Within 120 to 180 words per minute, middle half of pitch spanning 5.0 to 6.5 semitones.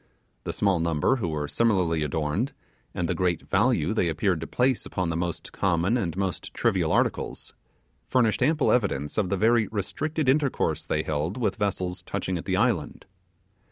Yes: average, 170 wpm; wide, 5.6 semitones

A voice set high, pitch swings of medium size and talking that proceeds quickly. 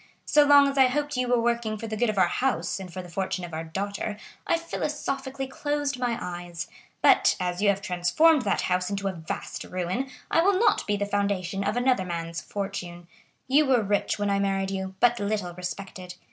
No: high, 200 Hz; wide, 5.8 semitones; fast, 210 wpm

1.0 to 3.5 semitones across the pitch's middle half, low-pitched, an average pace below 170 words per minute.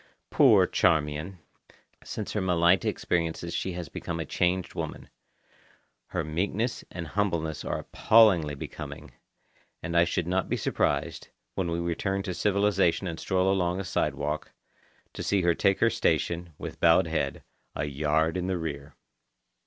Yes: average, 3.0 semitones; very low, 85 Hz; average, 150 wpm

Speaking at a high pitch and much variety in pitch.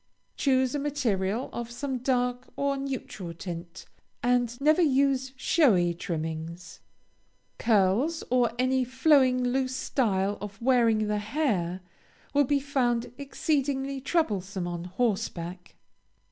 Yes: high, 245 Hz; wide, 5.7 semitones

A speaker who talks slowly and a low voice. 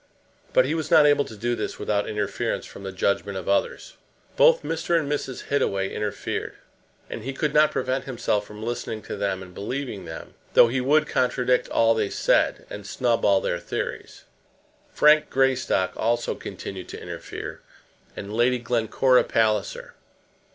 No: average, 165 wpm; low, 115 Hz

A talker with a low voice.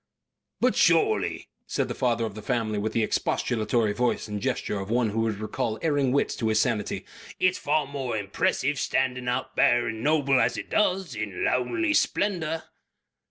Yes: low, 125 Hz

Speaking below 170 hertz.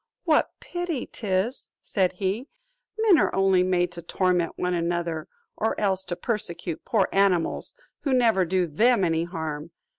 No: medium, 185 Hz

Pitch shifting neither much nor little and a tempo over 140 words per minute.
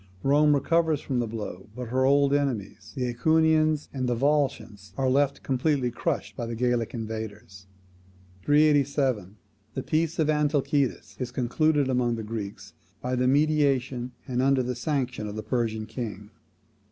Yes: average, 3.9 semitones; average, 150 wpm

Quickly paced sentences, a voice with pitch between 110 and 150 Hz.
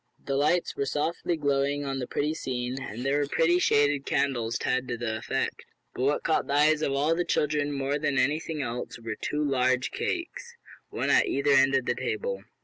Yes: fast, 210 wpm; medium, 140 Hz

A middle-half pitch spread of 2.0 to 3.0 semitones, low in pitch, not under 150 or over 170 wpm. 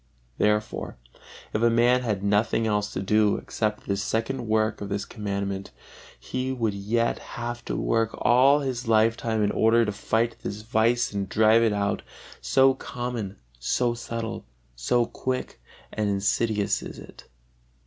Yes: narrow, 2.4 semitones; low, 110 Hz; average, 155 wpm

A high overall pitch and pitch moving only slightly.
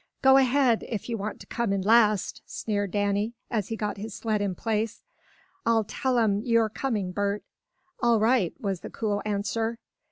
Yes: high, 215 Hz; narrow, 2.2 semitones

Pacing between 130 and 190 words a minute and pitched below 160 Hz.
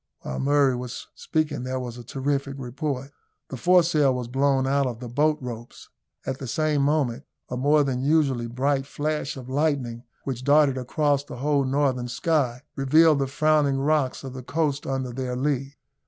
Yes: average, 175 wpm; low, 135 Hz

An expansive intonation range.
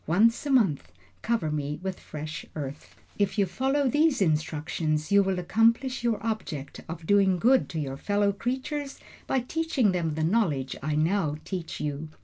Yes: wide, 7.1 semitones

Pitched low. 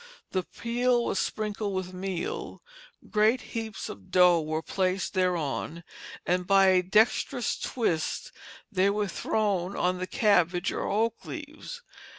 No: high, 190 Hz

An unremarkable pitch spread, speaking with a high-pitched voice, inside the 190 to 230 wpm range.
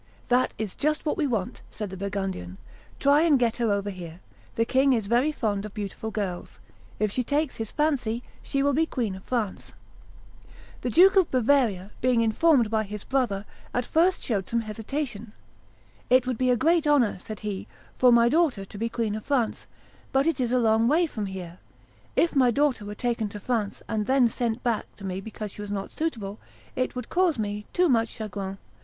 Yes: average, 4.5 semitones; high, 230 Hz; average, 200 wpm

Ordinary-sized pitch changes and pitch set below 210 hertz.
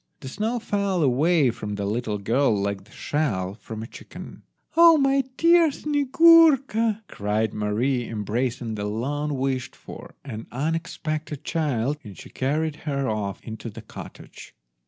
No: wide, 8.4 semitones; low, 135 Hz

